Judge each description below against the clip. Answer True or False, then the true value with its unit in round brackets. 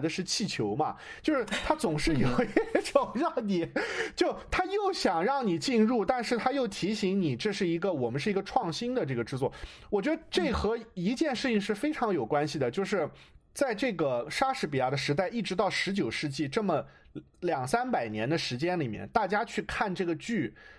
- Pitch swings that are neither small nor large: False (7.3 semitones)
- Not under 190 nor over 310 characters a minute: True (285 characters per minute)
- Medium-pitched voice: False (210 Hz)